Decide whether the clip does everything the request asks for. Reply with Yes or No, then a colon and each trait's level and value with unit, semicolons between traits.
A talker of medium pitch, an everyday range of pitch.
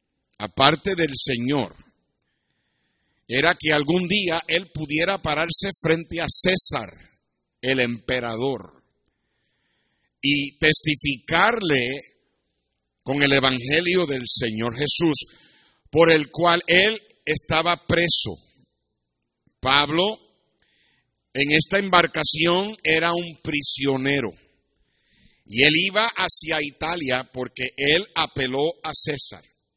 Yes: medium, 155 Hz; average, 4.1 semitones